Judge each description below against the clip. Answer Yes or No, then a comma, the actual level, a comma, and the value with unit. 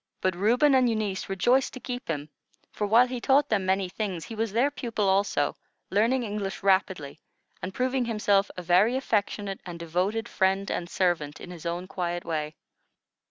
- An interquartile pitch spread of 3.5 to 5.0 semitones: Yes, average, 4.3 semitones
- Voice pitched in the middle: No, high, 195 Hz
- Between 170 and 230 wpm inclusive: Yes, average, 175 wpm